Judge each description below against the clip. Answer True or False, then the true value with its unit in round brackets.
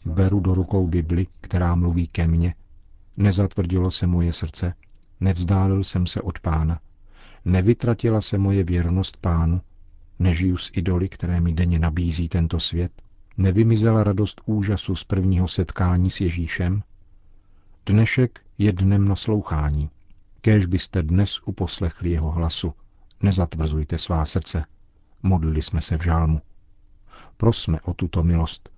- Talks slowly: False (125 wpm)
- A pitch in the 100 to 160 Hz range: False (90 Hz)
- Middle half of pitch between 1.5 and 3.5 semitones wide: True (2.6 semitones)